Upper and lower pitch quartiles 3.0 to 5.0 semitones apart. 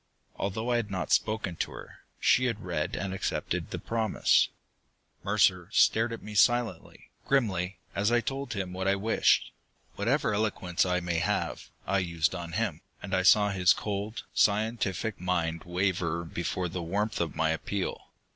Yes: average, 3.6 semitones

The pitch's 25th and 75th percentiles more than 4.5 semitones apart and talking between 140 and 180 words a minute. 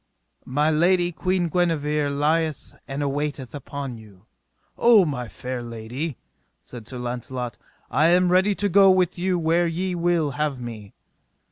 Yes: wide, 5.6 semitones; average, 145 wpm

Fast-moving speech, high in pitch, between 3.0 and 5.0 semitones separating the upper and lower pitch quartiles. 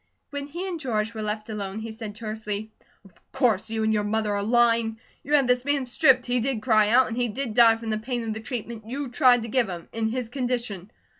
No: fast, 240 wpm; high, 230 Hz; narrow, 2.5 semitones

